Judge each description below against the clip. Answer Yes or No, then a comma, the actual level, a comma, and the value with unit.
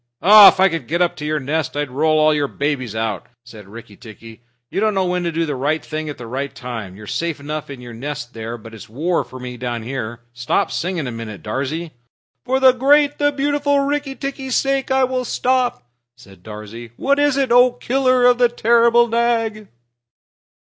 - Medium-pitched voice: Yes, medium, 155 Hz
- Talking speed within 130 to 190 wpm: No, fast, 205 wpm